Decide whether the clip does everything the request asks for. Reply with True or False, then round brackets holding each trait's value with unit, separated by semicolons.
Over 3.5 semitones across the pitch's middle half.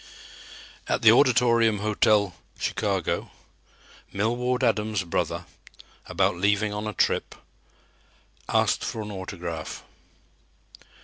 False (2.6 semitones)